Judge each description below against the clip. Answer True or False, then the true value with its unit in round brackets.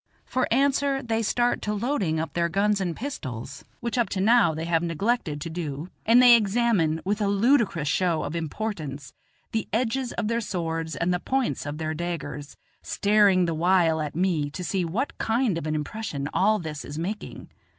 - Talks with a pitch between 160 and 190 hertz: True (185 Hz)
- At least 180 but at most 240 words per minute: True (190 wpm)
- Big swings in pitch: True (5.9 semitones)